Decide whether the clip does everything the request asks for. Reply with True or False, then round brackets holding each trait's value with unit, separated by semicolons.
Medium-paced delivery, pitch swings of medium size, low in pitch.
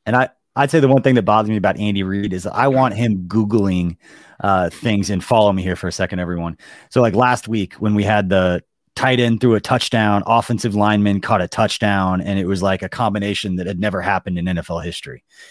False (230 wpm; 3.7 semitones; 105 Hz)